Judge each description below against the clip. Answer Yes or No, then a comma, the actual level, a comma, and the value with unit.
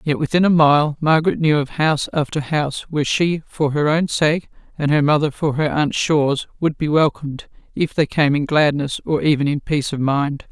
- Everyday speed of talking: No, fast, 210 wpm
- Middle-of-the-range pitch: Yes, medium, 150 Hz